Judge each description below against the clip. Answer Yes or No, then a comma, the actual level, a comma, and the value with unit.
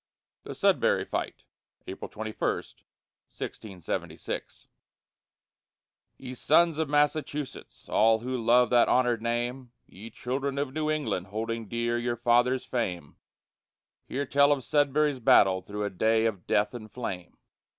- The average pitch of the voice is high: No, low, 120 Hz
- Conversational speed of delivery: No, slow, 130 wpm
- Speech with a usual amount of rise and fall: Yes, average, 3.8 semitones